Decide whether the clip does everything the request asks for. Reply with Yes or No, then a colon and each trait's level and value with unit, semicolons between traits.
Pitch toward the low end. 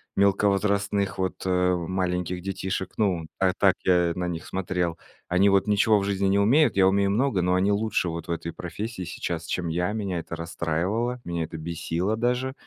Yes: very low, 95 Hz